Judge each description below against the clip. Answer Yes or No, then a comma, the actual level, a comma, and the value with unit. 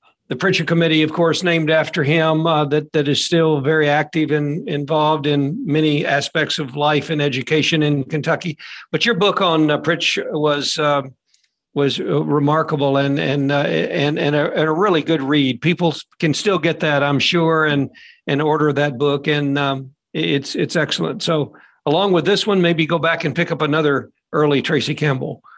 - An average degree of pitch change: No, narrow, 2.0 semitones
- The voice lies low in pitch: No, medium, 150 Hz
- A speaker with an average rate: Yes, average, 190 wpm